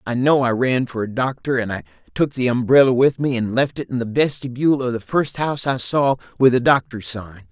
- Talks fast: Yes, fast, 240 wpm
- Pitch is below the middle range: Yes, low, 125 Hz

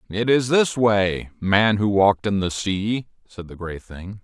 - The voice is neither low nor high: No, low, 105 Hz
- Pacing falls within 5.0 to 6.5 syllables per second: No, 4.0 syllables/s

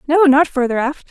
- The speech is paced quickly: Yes, fast, 220 wpm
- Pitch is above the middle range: Yes, very high, 285 Hz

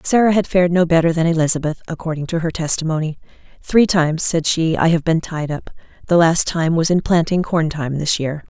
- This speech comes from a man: No, female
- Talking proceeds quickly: Yes, fast, 210 wpm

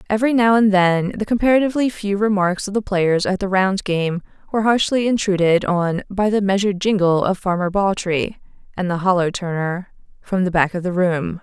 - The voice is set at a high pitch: Yes, high, 195 Hz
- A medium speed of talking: Yes, average, 190 wpm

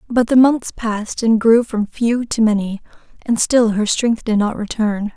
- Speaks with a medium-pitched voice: No, high, 225 Hz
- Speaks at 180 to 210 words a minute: Yes, average, 200 wpm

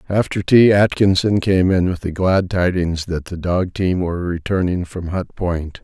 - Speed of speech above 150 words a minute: Yes, average, 185 wpm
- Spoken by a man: Yes, male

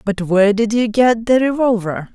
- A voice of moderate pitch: No, high, 220 Hz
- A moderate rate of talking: Yes, average, 195 wpm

